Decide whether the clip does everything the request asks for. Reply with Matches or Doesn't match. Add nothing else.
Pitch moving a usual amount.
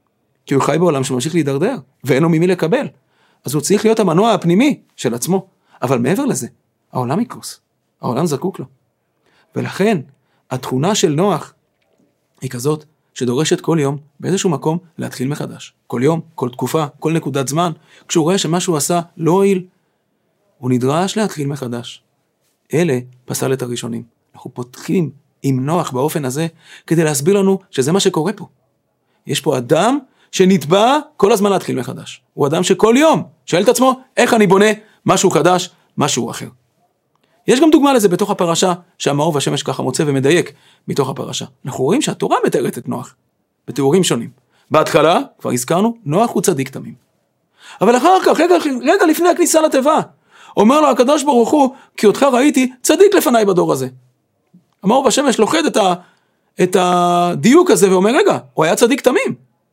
Doesn't match